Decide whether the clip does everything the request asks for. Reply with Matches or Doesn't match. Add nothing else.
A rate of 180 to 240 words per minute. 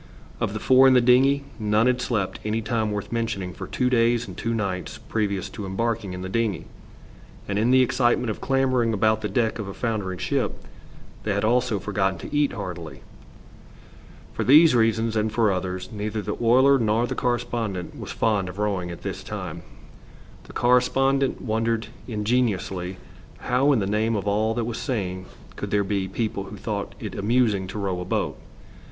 Matches